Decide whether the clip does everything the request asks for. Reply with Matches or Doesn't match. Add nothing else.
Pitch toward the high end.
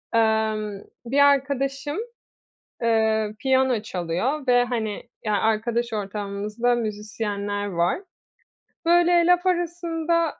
Matches